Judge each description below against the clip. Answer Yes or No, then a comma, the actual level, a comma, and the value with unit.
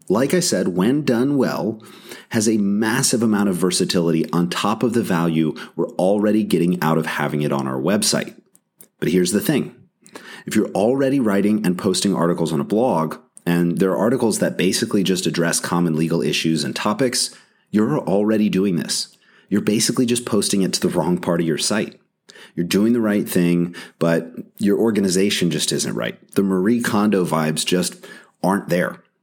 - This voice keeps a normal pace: Yes, average, 180 wpm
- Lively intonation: No, average, 4.5 semitones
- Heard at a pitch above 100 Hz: No, very low, 95 Hz